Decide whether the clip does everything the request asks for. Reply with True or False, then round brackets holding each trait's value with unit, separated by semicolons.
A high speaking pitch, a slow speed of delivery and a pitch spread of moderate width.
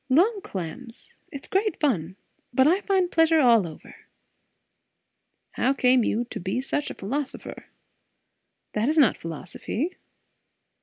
False (260 Hz; 125 wpm; 7.0 semitones)